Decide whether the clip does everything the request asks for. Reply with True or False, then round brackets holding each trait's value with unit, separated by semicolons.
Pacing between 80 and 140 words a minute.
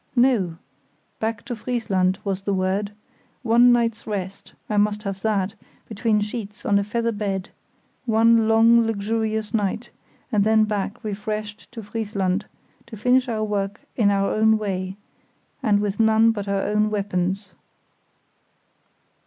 True (135 wpm)